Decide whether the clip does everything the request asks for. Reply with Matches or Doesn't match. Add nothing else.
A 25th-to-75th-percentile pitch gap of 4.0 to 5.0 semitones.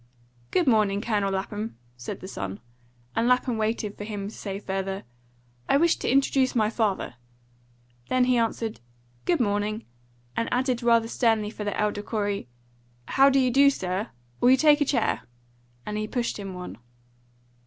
Doesn't match